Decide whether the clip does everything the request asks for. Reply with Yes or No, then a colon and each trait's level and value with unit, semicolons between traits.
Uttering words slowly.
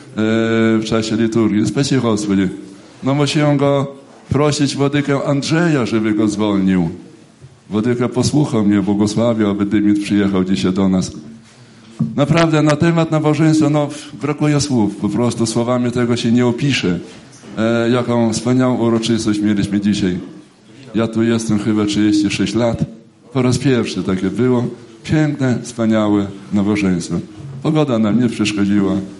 No: average, 125 wpm